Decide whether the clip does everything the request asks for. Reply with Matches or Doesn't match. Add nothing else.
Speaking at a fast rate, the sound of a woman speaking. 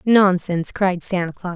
Doesn't match